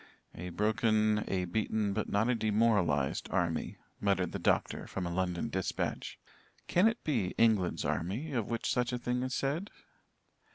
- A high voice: No, low, 110 Hz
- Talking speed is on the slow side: No, average, 160 wpm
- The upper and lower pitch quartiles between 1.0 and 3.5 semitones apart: No, average, 4.5 semitones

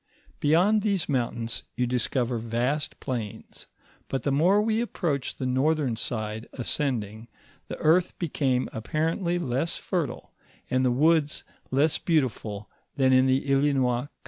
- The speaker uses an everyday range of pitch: Yes, average, 4.6 semitones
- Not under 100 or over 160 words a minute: Yes, average, 140 wpm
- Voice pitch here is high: No, low, 135 Hz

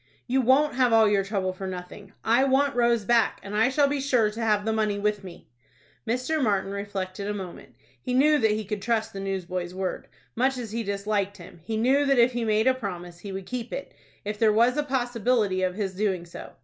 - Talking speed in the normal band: No, fast, 225 wpm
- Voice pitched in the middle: No, high, 215 Hz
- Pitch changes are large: No, average, 4.0 semitones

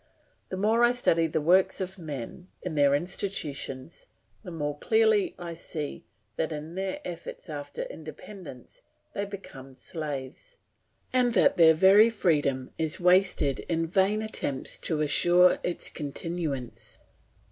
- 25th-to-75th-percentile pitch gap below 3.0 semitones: No, average, 4.8 semitones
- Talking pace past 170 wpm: No, slow, 135 wpm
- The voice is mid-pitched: Yes, medium, 170 Hz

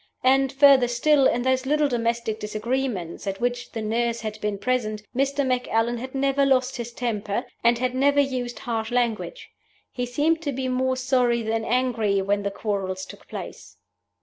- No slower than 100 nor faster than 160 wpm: No, average, 175 wpm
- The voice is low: No, high, 245 Hz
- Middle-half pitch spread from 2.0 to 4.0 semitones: Yes, average, 2.9 semitones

